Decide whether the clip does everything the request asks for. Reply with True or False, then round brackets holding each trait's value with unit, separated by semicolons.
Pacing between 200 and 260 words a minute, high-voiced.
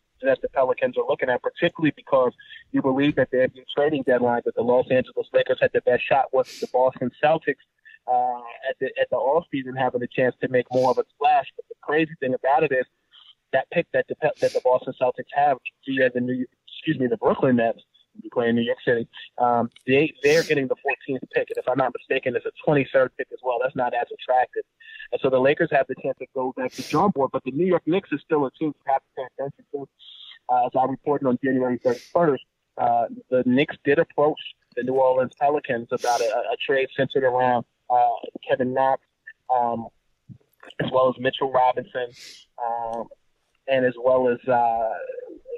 False (205 wpm; 135 Hz)